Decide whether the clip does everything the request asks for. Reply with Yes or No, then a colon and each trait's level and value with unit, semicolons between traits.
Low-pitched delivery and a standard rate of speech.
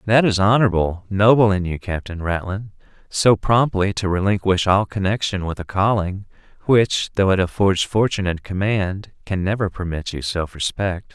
Yes: low, 100 Hz; average, 160 wpm